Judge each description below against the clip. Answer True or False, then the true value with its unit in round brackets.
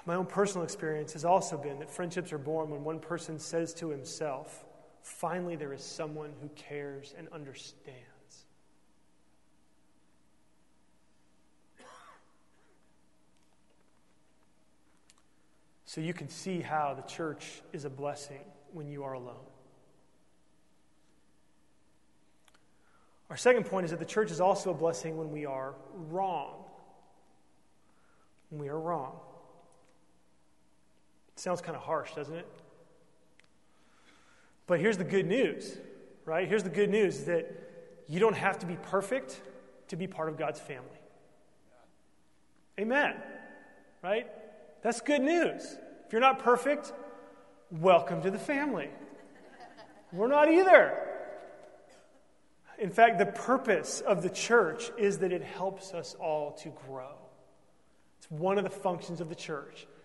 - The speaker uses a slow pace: True (125 wpm)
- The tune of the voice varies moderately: True (4.8 semitones)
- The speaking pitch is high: False (170 Hz)